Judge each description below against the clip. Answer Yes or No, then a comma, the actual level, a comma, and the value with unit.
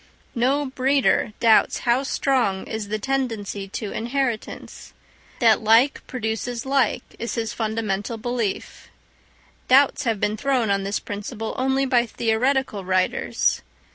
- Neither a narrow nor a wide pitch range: Yes, average, 3.5 semitones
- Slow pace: Yes, slow, 125 wpm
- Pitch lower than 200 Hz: No, high, 230 Hz